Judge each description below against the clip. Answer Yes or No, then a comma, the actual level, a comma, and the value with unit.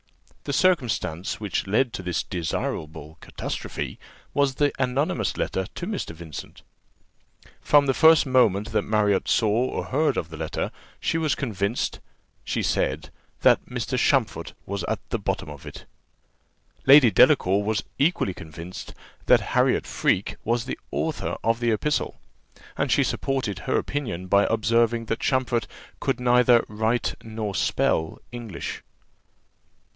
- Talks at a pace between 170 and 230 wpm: No, average, 140 wpm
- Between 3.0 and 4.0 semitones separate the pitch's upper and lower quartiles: No, average, 5.1 semitones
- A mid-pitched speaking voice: No, low, 115 Hz